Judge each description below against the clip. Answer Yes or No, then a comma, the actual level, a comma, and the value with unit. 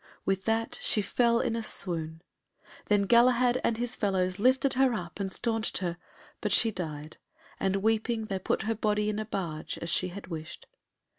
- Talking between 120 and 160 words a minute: No, average, 180 wpm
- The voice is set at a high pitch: Yes, high, 210 Hz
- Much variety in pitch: No, average, 3.9 semitones